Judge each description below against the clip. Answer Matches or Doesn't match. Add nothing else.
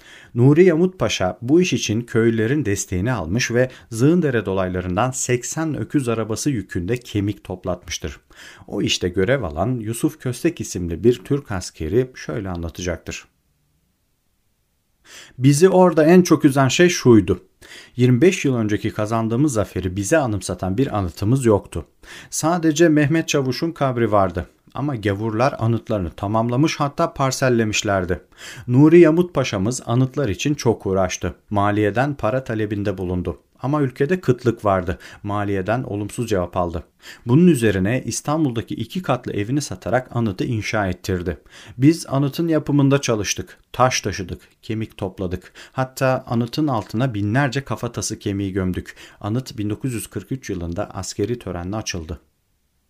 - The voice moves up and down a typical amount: Doesn't match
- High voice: Doesn't match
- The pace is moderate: Matches